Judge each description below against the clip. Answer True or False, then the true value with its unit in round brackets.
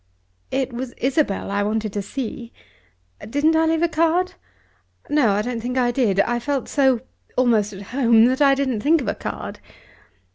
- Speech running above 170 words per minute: True (180 wpm)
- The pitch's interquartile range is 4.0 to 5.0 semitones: True (4.3 semitones)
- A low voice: False (250 Hz)